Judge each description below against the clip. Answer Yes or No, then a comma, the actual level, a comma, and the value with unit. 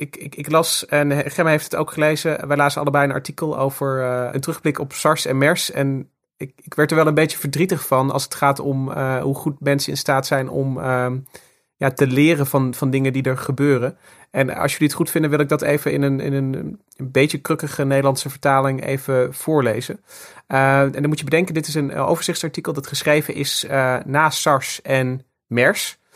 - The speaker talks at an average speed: No, fast, 215 wpm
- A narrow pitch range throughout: Yes, narrow, 2.2 semitones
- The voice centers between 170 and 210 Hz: No, medium, 140 Hz